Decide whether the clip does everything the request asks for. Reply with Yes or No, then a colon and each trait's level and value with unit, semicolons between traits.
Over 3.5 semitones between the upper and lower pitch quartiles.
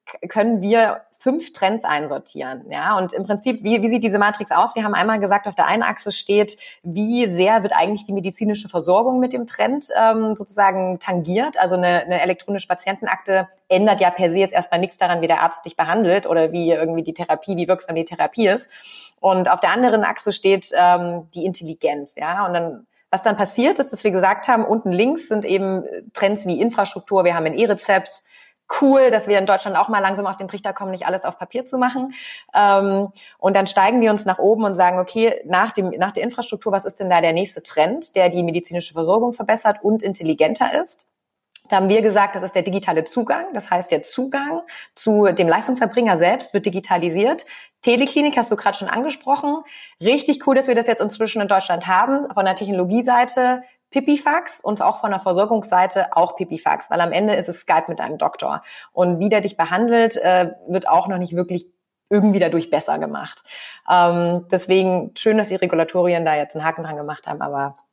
Yes: average, 3.9 semitones